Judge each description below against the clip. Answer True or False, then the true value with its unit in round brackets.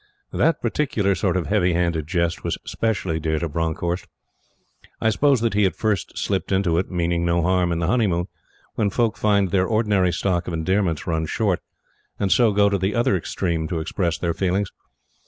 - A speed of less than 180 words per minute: False (190 wpm)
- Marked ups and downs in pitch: False (3.4 semitones)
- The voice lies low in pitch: True (95 Hz)